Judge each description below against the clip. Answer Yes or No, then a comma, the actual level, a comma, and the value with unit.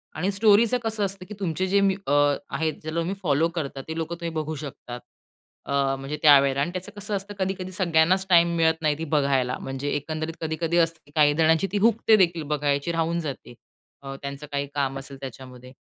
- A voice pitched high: No, medium, 160 Hz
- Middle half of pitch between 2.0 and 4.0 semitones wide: No, average, 4.5 semitones